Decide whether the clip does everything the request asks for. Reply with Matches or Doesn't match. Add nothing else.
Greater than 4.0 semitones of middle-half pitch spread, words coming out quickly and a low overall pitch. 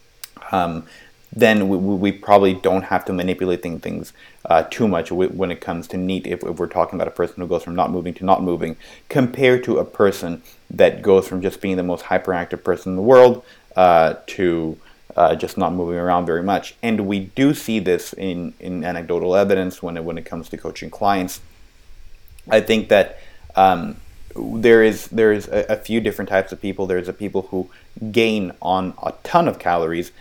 Doesn't match